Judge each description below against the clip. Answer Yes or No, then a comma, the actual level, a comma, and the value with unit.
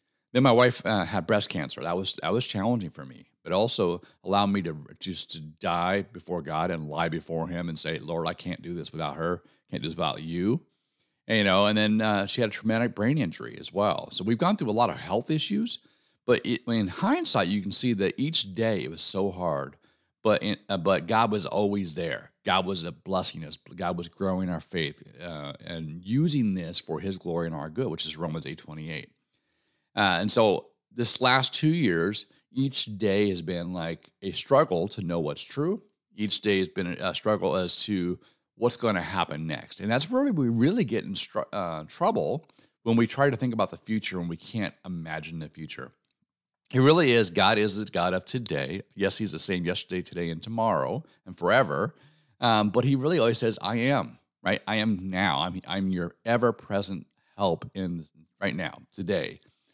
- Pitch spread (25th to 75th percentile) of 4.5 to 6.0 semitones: Yes, average, 5.3 semitones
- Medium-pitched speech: No, low, 100 Hz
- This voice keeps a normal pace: No, fast, 210 wpm